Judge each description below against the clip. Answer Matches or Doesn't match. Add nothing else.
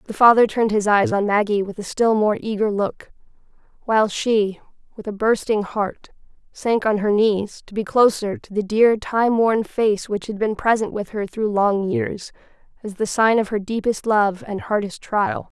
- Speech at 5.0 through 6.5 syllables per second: Doesn't match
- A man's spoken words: Doesn't match